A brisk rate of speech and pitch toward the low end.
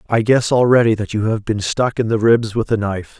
Yes: fast, 265 wpm; low, 110 Hz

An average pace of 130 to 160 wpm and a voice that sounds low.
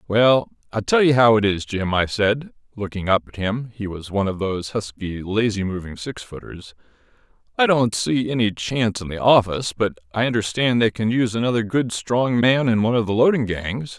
No: average, 195 wpm; low, 110 Hz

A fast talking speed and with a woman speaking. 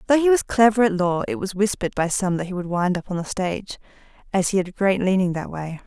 Yes: fast, 275 wpm; female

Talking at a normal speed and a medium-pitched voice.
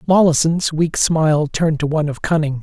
Yes: average, 185 wpm; medium, 155 Hz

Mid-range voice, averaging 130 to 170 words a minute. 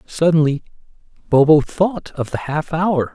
Yes: medium, 160 Hz; slow, 135 wpm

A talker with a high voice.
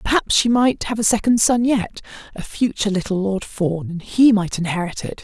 Yes: high, 210 Hz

